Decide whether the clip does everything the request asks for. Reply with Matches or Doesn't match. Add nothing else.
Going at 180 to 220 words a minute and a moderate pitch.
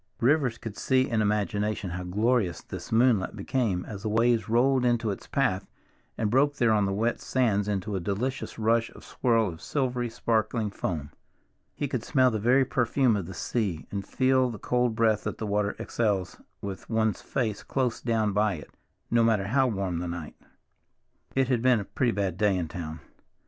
Doesn't match